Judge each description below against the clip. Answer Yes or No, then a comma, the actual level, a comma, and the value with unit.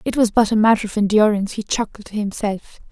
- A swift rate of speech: Yes, fast, 225 wpm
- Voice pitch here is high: Yes, high, 210 Hz